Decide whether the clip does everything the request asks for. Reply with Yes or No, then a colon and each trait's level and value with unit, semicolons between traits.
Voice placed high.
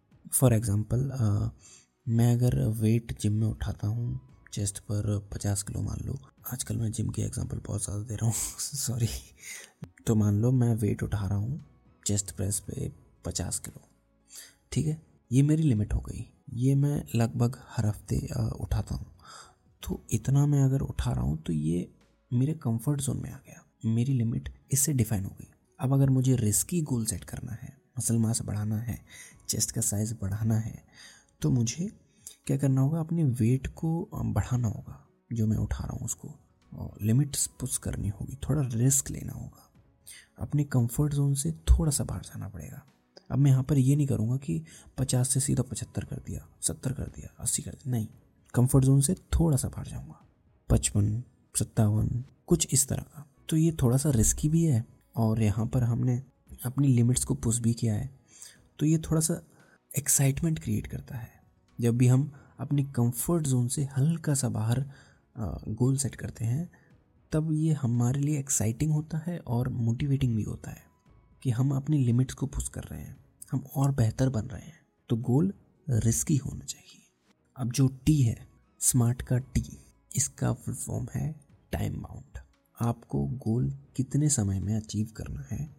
No: low, 125 Hz